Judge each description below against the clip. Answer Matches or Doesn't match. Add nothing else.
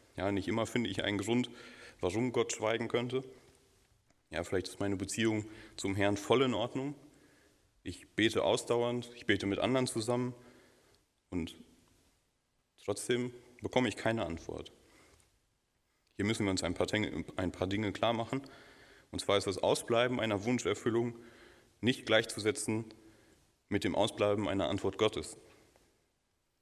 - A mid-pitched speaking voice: Doesn't match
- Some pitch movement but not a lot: Matches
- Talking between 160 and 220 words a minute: Doesn't match